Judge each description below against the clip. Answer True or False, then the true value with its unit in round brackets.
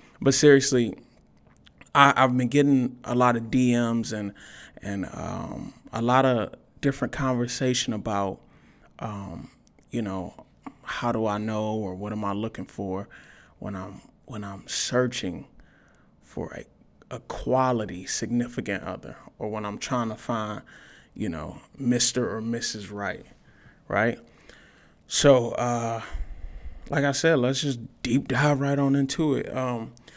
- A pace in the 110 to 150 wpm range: True (140 wpm)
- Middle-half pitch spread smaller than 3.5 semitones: False (3.8 semitones)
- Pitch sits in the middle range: False (120 Hz)